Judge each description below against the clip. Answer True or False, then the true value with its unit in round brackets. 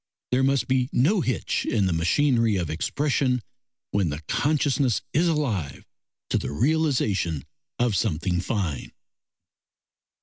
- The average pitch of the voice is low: True (120 Hz)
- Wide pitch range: True (7.7 semitones)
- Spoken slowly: True (125 wpm)